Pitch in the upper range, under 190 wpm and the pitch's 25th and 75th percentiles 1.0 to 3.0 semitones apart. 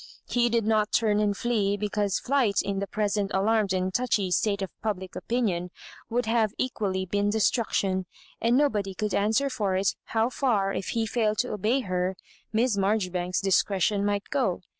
Yes: high, 205 Hz; average, 175 wpm; average, 2.7 semitones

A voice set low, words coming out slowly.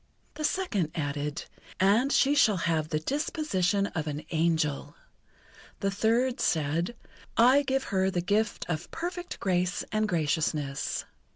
No: high, 190 Hz; slow, 130 wpm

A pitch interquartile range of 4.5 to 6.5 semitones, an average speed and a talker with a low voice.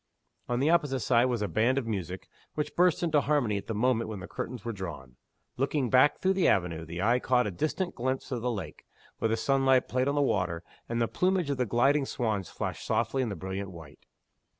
No: wide, 5.4 semitones; fast, 220 wpm; low, 120 Hz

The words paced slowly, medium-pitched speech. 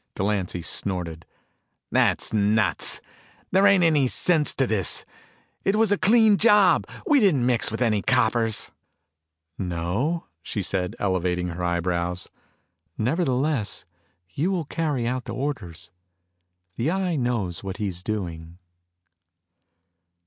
No: slow, 120 wpm; low, 115 Hz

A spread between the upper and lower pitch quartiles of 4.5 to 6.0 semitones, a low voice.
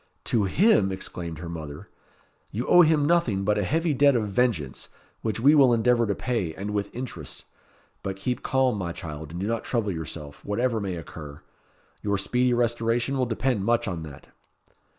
Yes: average, 5.3 semitones; low, 110 Hz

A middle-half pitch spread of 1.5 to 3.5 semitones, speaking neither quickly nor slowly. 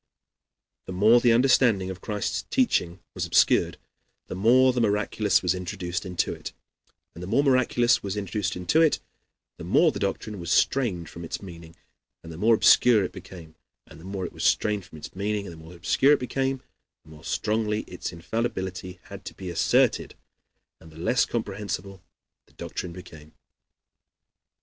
No: average, 4.6 semitones; average, 175 wpm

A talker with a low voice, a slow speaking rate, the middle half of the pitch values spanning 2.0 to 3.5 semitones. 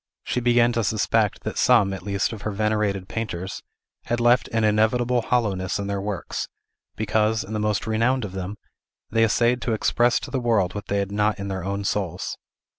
No: low, 105 Hz; average, 195 wpm; average, 2.8 semitones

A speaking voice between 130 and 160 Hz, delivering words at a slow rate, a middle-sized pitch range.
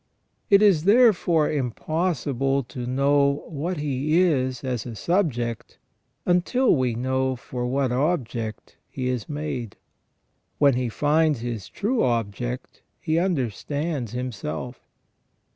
Yes: low, 135 Hz; slow, 125 wpm; average, 4.4 semitones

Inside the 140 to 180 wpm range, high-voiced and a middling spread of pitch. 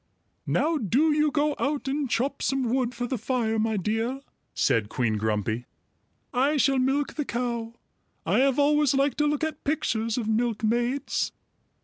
Yes: average, 160 wpm; very high, 255 Hz; average, 4.2 semitones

